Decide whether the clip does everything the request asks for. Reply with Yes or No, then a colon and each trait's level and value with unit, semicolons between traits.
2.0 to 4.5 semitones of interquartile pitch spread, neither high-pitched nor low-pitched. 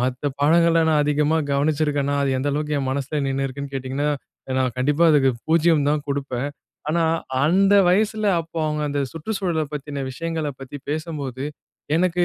Yes: average, 2.9 semitones; medium, 150 Hz